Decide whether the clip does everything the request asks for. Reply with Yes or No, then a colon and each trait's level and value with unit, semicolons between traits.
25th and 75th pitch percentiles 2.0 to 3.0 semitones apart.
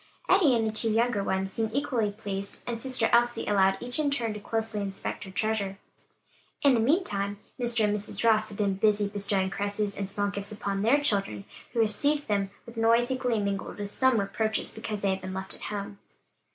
Yes: average, 2.7 semitones